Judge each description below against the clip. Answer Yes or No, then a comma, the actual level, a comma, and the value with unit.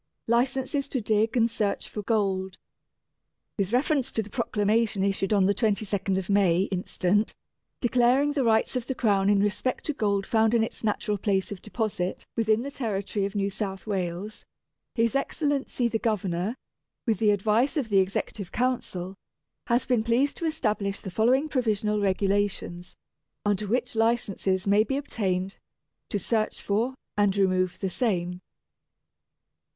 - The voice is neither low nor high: No, high, 210 Hz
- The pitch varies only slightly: No, average, 3.3 semitones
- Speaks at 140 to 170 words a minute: Yes, average, 155 wpm